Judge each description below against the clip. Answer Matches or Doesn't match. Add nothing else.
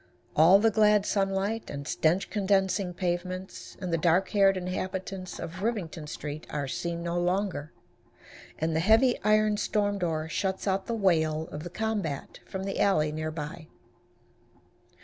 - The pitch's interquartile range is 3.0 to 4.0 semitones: Matches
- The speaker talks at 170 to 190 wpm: Doesn't match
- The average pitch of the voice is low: Doesn't match